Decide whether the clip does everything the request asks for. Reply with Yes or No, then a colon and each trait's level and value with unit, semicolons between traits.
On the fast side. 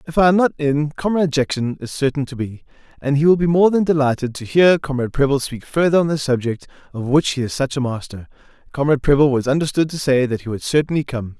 Yes: fast, 235 wpm